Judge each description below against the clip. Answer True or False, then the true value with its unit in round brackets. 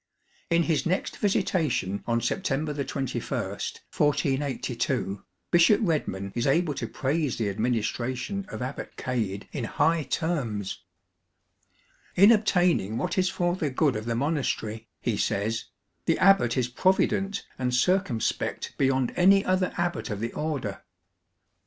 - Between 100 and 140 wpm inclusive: True (135 wpm)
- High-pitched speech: False (135 Hz)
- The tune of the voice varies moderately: False (6.8 semitones)